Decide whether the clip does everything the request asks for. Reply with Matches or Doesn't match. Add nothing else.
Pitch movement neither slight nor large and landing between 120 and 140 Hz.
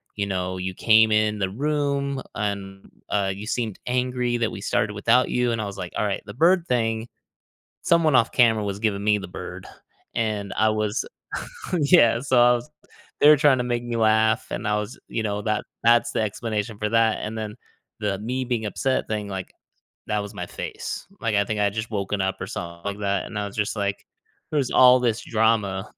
Doesn't match